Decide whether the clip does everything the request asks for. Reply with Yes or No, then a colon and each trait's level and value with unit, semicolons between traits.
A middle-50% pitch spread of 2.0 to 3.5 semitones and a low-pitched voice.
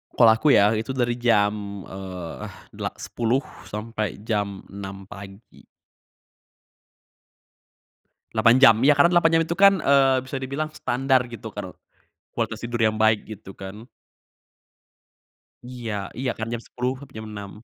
No: average, 4.1 semitones; low, 115 Hz